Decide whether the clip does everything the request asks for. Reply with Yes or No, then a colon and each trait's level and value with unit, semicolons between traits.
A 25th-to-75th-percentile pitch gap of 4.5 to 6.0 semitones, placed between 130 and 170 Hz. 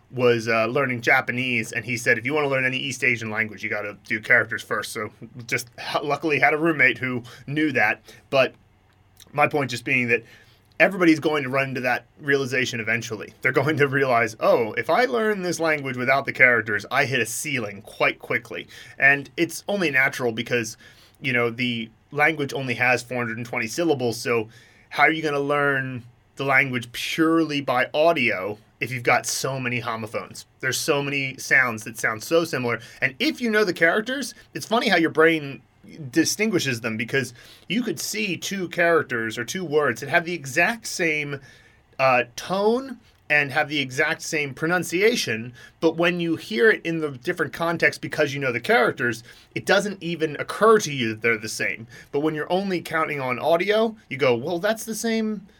Yes: wide, 5.4 semitones; medium, 140 Hz